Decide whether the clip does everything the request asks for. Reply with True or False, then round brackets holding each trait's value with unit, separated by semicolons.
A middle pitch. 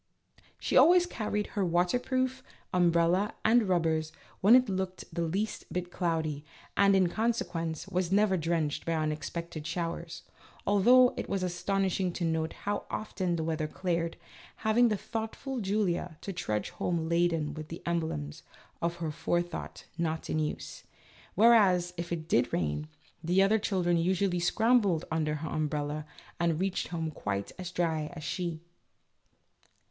True (175 Hz)